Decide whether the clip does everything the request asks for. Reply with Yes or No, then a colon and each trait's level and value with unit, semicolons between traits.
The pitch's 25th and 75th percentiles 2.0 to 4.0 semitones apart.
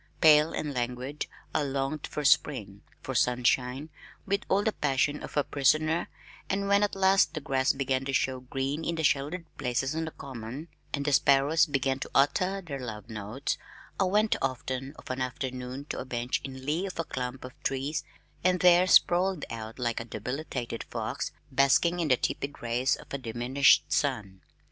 Yes: average, 3.7 semitones